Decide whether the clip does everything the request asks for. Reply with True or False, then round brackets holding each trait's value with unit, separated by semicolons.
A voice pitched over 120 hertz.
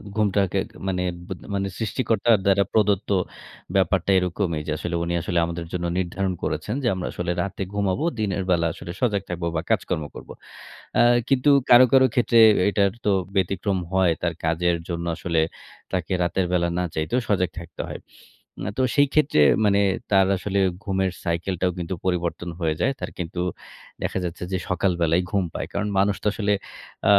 False (95 Hz)